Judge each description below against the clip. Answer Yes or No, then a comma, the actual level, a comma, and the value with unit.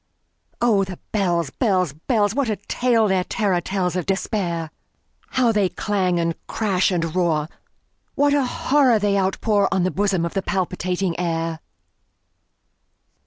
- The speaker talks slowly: Yes, slow, 120 wpm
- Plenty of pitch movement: No, average, 3.3 semitones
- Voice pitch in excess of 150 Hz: Yes, high, 190 Hz